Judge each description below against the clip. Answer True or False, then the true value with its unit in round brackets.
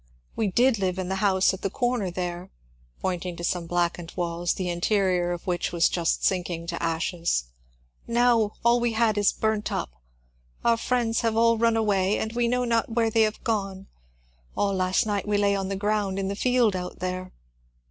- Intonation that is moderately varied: True (3.9 semitones)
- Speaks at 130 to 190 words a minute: False (200 wpm)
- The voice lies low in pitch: False (195 Hz)